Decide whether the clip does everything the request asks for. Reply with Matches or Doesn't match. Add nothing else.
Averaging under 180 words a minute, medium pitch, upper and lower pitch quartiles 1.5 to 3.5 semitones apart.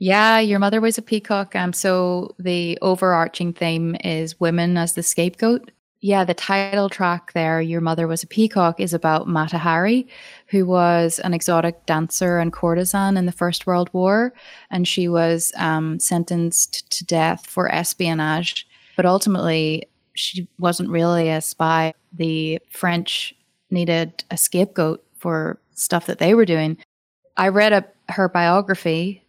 Matches